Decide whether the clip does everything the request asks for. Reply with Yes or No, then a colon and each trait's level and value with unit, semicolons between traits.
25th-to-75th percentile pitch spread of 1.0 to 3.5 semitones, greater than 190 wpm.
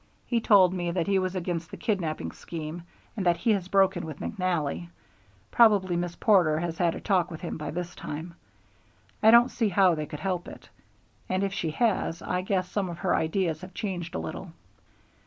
Yes: average, 2.8 semitones; average, 200 wpm